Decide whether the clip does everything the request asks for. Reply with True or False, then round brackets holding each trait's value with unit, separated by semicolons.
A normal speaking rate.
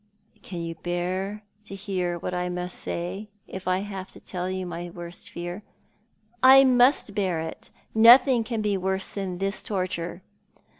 True (170 wpm)